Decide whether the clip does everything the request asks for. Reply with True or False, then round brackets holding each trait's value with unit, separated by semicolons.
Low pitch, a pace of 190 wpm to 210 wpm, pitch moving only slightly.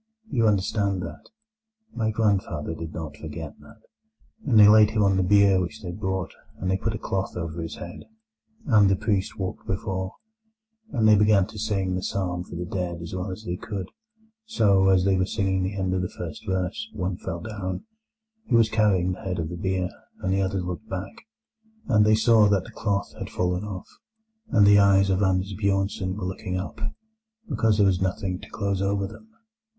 True (95 Hz; 200 wpm; 2.2 semitones)